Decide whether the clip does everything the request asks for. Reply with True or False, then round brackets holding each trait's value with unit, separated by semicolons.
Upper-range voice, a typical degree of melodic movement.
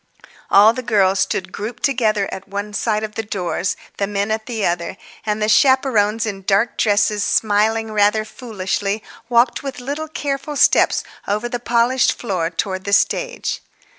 True (215 Hz; 3.0 semitones)